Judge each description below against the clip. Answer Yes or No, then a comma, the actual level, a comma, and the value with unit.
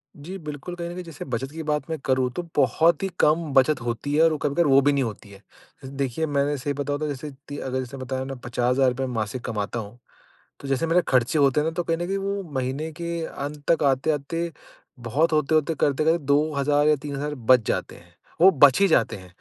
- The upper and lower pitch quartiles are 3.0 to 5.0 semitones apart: Yes, average, 3.5 semitones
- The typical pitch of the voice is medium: Yes, medium, 145 Hz